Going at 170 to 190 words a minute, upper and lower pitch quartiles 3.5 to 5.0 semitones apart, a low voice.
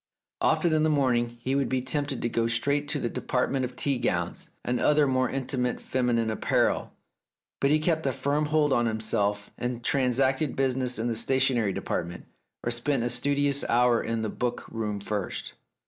No: average, 180 wpm; average, 3.1 semitones; low, 125 Hz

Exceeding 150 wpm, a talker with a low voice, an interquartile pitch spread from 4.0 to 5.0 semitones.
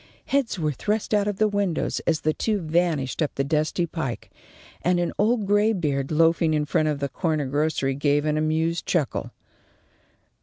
No: average, 175 wpm; medium, 160 Hz; average, 4.3 semitones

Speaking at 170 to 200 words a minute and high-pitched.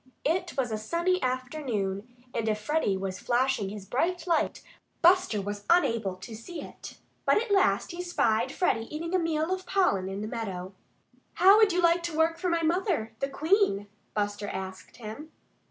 Yes: average, 180 wpm; very high, 265 Hz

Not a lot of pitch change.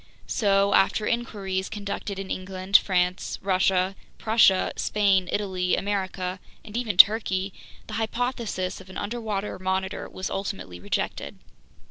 Yes: narrow, 2.0 semitones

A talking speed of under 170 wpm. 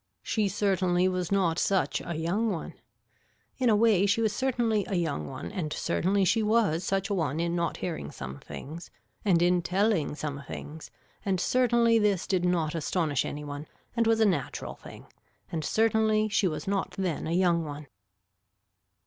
No: average, 175 wpm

